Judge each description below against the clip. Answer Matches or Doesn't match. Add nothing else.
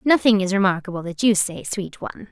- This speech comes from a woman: Matches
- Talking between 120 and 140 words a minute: Doesn't match